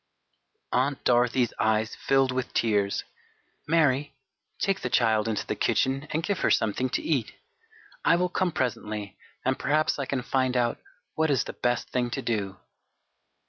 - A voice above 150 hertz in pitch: No, low, 130 Hz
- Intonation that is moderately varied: Yes, average, 4.1 semitones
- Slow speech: No, average, 160 wpm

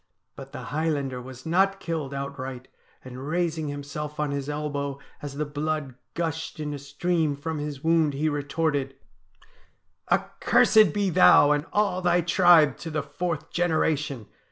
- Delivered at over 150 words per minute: Yes, average, 160 wpm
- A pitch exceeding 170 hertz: No, medium, 150 Hz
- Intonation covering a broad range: No, narrow, 2.6 semitones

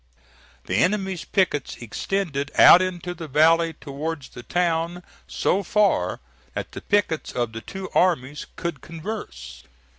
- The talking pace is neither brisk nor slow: No, slow, 130 wpm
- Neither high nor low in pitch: Yes, medium, 165 Hz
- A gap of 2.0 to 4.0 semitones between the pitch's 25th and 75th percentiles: No, average, 4.5 semitones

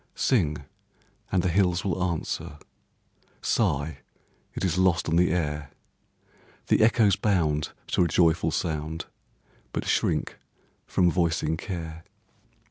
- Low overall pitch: Yes, very low, 85 Hz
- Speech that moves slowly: Yes, slow, 120 wpm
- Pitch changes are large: No, average, 2.7 semitones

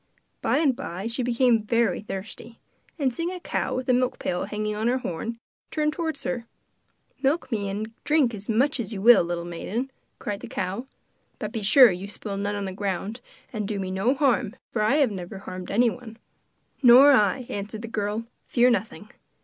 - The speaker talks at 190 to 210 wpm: Yes, average, 195 wpm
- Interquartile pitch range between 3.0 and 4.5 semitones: Yes, average, 4.0 semitones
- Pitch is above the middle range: Yes, high, 225 Hz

